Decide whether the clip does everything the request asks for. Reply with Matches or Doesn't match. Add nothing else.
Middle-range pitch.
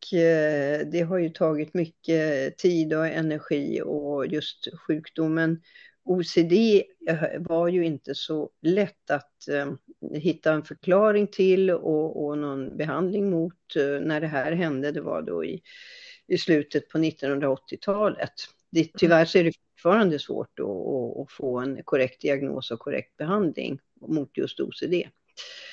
Matches